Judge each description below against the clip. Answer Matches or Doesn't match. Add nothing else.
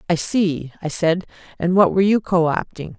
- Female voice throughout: Matches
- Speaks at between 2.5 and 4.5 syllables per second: Doesn't match